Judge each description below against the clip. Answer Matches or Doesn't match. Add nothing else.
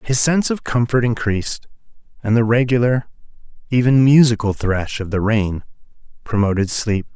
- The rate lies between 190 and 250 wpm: Doesn't match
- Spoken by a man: Matches